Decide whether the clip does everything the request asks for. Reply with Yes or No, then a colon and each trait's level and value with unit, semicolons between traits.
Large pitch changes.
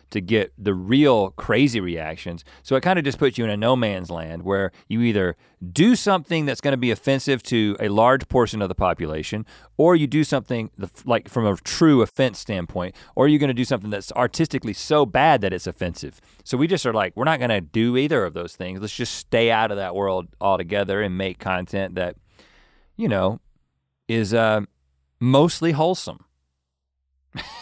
Yes: wide, 6.3 semitones